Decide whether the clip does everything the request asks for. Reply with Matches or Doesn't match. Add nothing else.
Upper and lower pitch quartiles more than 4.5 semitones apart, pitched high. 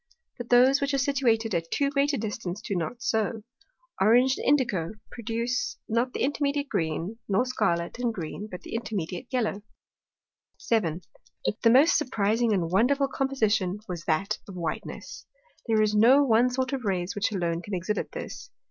Matches